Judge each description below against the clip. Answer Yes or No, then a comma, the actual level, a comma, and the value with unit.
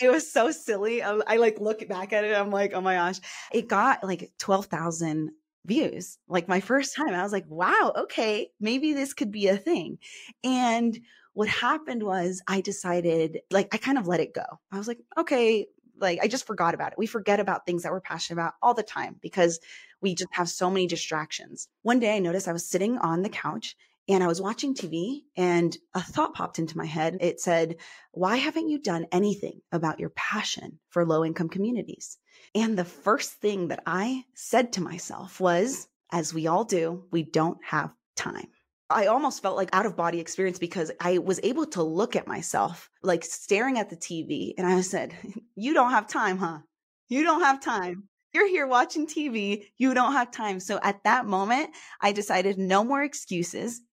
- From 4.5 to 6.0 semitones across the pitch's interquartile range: Yes, wide, 5.4 semitones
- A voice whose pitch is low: No, high, 200 Hz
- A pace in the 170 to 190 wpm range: No, average, 200 wpm